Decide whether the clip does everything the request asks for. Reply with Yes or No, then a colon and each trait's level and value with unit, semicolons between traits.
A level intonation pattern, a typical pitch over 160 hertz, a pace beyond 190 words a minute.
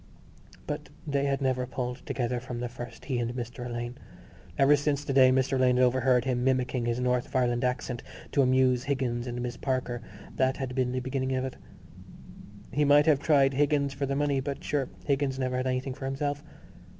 No: narrow, 1.8 semitones; low, 130 Hz; average, 200 wpm